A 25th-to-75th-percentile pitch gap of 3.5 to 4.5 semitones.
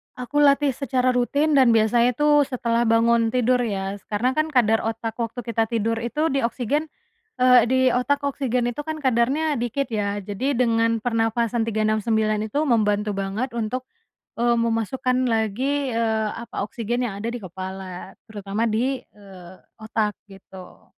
No: average, 2.8 semitones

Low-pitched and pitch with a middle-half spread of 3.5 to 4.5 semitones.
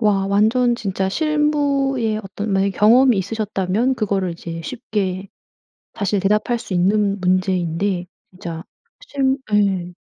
No: high, 205 Hz; average, 4.0 semitones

